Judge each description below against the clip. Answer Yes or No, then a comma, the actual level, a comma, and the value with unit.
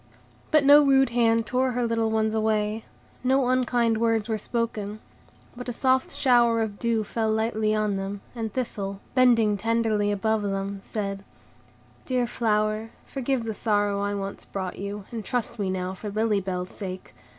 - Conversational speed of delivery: Yes, average, 165 wpm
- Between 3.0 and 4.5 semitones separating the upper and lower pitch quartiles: No, narrow, 2.6 semitones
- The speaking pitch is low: No, high, 220 Hz